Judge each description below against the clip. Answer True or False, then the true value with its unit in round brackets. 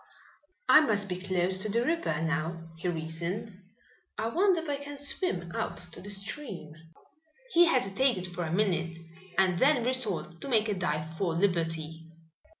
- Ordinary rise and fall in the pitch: False (6.5 semitones)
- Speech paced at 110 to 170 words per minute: True (160 wpm)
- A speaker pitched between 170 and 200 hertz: True (190 Hz)